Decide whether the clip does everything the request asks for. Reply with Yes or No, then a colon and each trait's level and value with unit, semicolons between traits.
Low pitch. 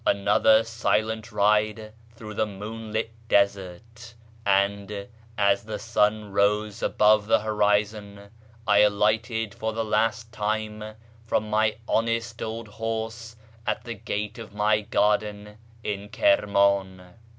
Yes: low, 105 Hz